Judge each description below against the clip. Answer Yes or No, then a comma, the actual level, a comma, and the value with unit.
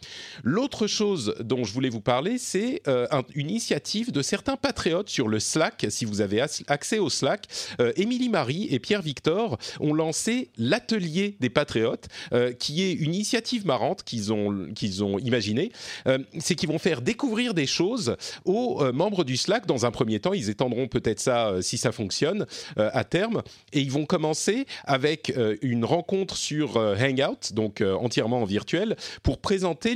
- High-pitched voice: No, medium, 140 Hz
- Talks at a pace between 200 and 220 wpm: No, average, 160 wpm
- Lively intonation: Yes, wide, 8.3 semitones